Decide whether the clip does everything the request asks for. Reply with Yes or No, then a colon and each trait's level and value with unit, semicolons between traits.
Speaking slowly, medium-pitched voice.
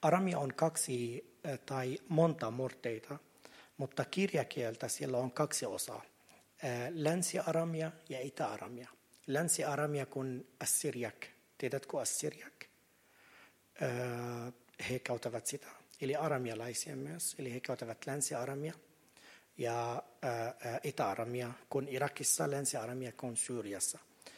No: slow, 90 wpm; low, 130 Hz